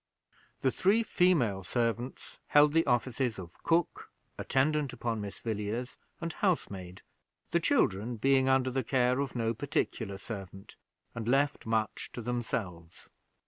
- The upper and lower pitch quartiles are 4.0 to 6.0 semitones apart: Yes, average, 4.3 semitones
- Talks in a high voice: No, low, 120 Hz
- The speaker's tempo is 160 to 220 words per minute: No, slow, 135 wpm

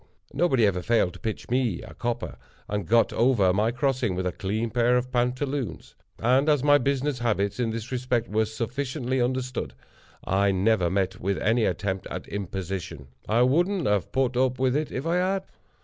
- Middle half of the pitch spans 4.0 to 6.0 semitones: Yes, average, 4.5 semitones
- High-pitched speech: No, low, 120 Hz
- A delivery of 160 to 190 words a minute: Yes, average, 180 wpm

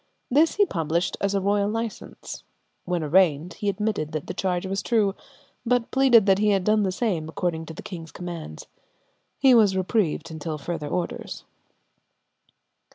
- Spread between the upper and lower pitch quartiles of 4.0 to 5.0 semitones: Yes, average, 4.4 semitones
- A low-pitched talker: No, high, 190 Hz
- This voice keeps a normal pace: Yes, average, 160 wpm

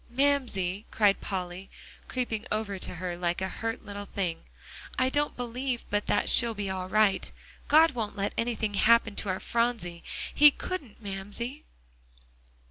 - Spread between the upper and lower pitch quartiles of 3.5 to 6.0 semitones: Yes, average, 4.1 semitones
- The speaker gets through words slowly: No, average, 150 wpm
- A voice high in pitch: Yes, high, 215 Hz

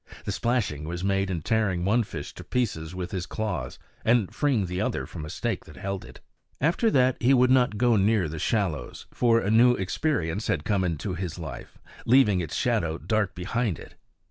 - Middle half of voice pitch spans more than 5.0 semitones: Yes, wide, 5.4 semitones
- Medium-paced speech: Yes, average, 195 wpm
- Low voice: Yes, low, 100 Hz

